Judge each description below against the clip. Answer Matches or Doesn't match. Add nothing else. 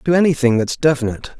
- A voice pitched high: Doesn't match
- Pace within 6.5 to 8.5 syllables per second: Matches